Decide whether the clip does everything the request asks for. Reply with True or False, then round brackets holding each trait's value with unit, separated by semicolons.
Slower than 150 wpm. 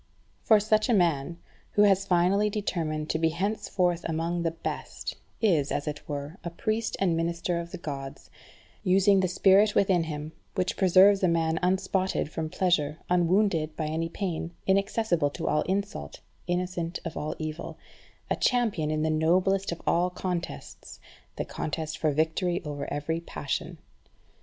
False (155 wpm)